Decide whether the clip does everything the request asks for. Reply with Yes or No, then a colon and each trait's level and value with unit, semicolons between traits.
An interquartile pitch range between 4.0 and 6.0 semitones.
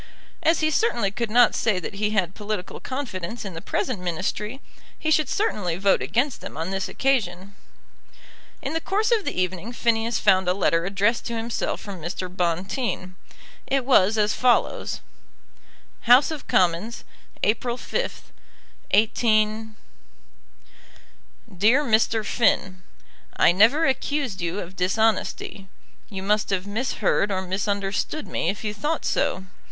Yes: average, 4.4 semitones